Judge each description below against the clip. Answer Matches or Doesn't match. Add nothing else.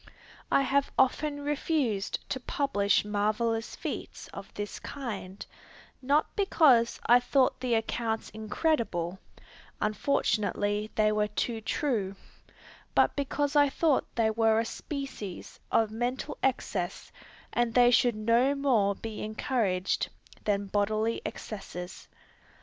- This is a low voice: Doesn't match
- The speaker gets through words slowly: Matches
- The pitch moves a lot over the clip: Doesn't match